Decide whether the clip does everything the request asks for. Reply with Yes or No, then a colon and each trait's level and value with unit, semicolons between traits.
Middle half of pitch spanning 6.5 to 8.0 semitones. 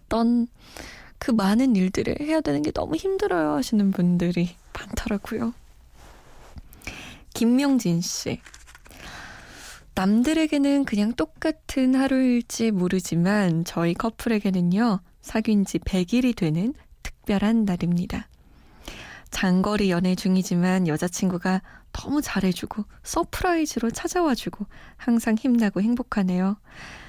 No: average, 5.2 semitones